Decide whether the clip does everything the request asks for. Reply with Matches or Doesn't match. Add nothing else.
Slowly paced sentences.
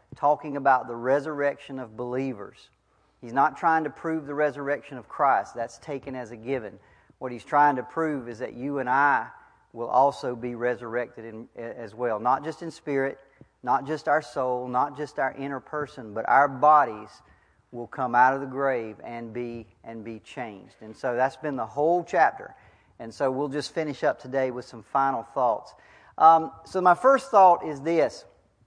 Doesn't match